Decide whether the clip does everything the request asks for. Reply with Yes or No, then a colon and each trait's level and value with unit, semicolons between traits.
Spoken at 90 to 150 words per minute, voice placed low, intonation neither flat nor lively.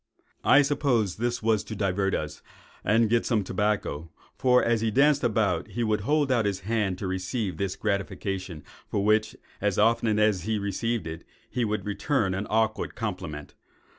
No: average, 170 wpm; low, 105 Hz; average, 3.1 semitones